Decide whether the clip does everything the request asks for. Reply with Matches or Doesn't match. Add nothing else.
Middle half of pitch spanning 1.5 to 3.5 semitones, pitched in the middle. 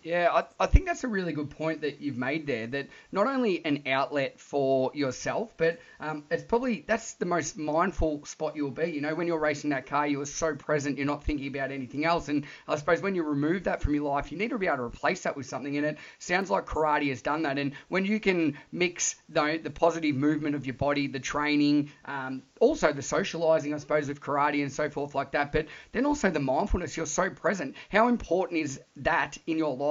Matches